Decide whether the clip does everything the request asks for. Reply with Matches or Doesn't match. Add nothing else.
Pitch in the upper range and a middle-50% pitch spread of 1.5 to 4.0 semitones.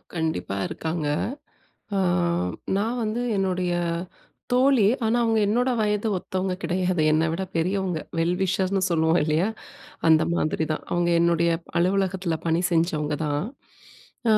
Doesn't match